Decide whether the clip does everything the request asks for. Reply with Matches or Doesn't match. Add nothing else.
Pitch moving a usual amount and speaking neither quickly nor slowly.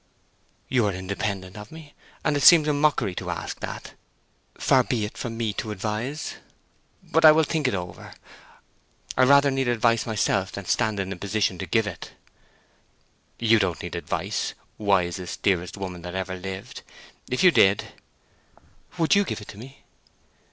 Doesn't match